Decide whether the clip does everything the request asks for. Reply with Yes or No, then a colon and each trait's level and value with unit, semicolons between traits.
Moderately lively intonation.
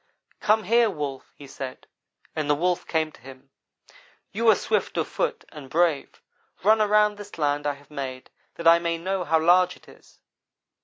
No: wide, 6.1 semitones